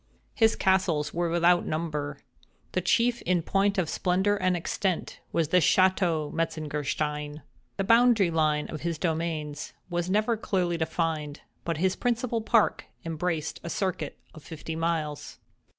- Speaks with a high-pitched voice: No, medium, 170 Hz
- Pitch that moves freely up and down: No, average, 3.4 semitones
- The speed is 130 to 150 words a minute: Yes, average, 140 wpm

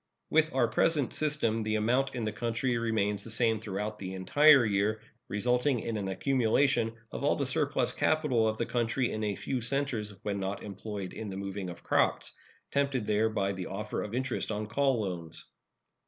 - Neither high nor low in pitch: No, low, 110 Hz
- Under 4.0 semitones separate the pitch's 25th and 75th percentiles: Yes, average, 3.6 semitones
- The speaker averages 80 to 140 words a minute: No, average, 185 wpm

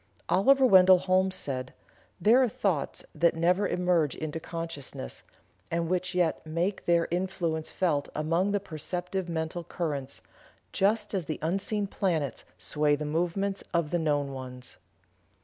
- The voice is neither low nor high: Yes, medium, 170 Hz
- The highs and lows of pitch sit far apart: No, average, 3.5 semitones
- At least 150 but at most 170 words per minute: No, average, 140 wpm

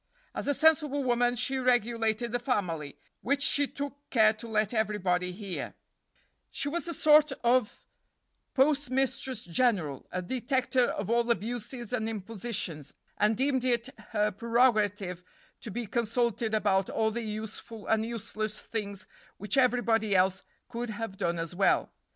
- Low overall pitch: No, high, 225 Hz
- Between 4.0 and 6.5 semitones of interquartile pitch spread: No, average, 3.3 semitones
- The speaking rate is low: No, average, 145 wpm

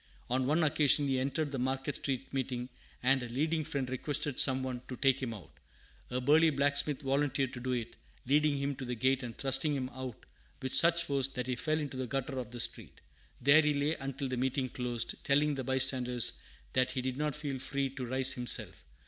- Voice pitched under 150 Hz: Yes, low, 135 Hz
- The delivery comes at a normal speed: No, fast, 210 wpm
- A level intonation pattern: Yes, narrow, 2.0 semitones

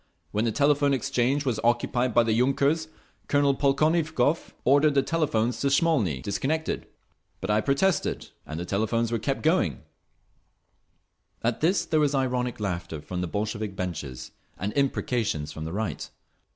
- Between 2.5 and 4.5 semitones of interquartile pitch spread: No, wide, 5.4 semitones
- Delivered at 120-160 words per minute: Yes, average, 150 wpm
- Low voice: Yes, low, 125 Hz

